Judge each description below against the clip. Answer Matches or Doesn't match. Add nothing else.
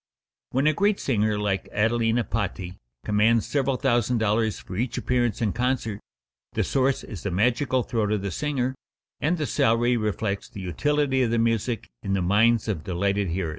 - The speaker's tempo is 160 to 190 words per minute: Matches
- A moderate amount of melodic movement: Matches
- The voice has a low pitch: Matches